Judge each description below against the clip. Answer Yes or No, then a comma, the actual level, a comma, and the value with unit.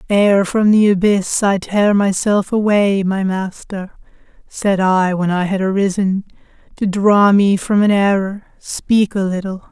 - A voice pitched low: No, high, 195 Hz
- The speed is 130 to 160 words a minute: Yes, average, 155 wpm